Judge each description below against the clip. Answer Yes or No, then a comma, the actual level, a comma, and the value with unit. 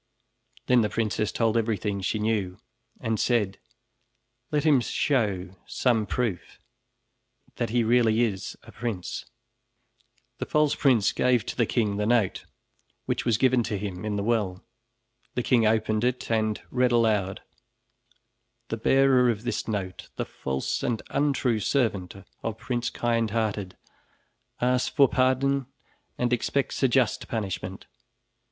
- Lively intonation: No, average, 3.1 semitones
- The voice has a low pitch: Yes, low, 115 Hz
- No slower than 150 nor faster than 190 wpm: No, slow, 135 wpm